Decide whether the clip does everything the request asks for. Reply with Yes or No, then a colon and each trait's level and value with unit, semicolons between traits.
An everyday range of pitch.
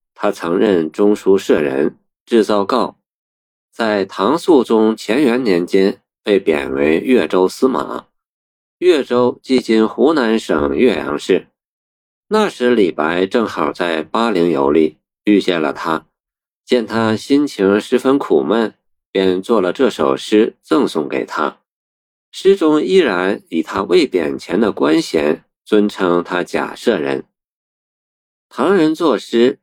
No: wide, 6.4 semitones